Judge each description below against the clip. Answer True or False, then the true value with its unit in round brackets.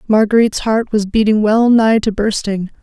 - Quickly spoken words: False (170 wpm)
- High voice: True (215 Hz)